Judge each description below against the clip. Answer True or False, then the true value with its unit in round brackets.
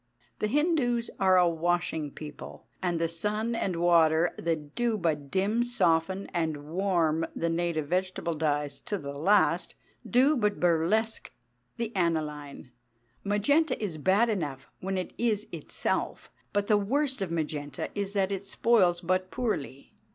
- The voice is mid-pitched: True (180 Hz)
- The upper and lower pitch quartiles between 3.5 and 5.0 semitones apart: True (4.6 semitones)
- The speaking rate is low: False (145 wpm)